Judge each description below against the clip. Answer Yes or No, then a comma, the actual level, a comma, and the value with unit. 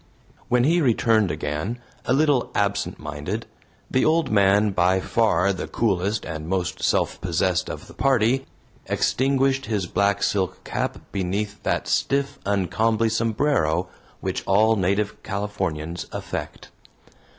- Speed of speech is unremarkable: No, slow, 130 wpm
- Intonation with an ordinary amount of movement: Yes, average, 4.2 semitones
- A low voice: Yes, low, 100 Hz